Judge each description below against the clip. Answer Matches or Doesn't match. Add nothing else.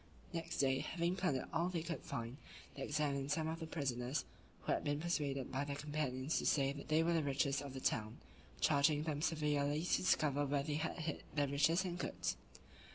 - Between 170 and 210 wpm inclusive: Matches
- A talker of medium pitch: Matches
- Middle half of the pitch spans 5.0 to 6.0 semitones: Doesn't match